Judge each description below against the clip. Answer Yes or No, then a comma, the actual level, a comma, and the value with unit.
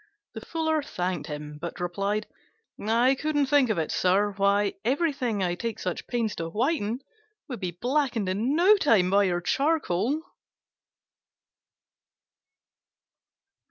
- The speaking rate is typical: No, slow, 125 wpm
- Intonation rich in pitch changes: Yes, wide, 7.1 semitones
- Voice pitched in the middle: No, high, 215 Hz